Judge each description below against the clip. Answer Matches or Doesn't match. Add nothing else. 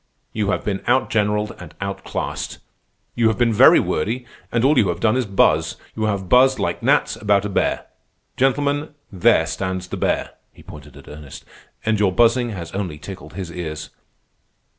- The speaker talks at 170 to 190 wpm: Matches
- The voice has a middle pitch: Doesn't match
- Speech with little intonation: Doesn't match